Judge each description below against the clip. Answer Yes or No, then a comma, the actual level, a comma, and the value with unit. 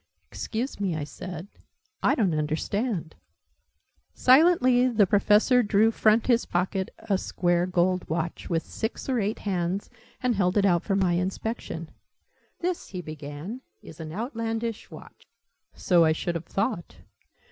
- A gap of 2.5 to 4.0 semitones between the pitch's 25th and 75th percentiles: No, average, 4.8 semitones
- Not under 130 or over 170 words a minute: Yes, average, 145 wpm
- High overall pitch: Yes, high, 195 Hz